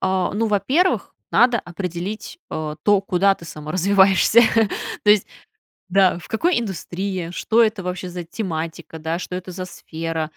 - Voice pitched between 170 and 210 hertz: Yes, medium, 185 Hz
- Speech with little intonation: No, average, 3.2 semitones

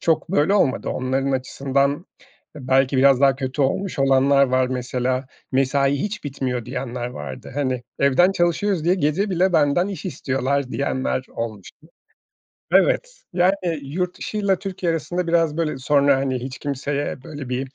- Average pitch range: Yes, average, 4.6 semitones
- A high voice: No, medium, 140 Hz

